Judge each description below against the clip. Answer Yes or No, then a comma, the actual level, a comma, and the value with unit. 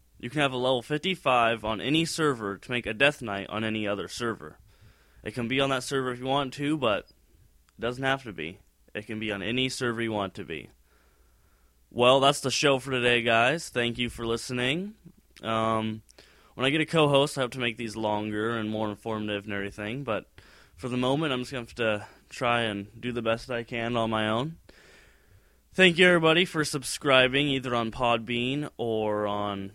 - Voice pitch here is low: Yes, low, 120 Hz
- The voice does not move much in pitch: No, average, 3.8 semitones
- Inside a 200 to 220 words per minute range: Yes, fast, 205 wpm